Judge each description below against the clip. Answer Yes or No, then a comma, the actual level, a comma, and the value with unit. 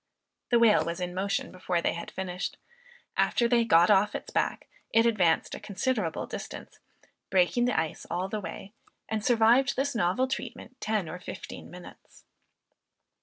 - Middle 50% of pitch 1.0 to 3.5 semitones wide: No, average, 4.6 semitones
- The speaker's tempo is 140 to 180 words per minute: Yes, average, 160 wpm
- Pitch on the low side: No, high, 205 Hz